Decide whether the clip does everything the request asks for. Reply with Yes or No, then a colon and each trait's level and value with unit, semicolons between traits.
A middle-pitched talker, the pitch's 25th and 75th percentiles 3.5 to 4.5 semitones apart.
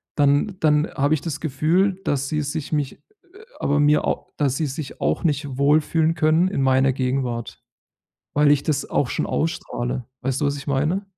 No: medium, 145 Hz; narrow, 2.6 semitones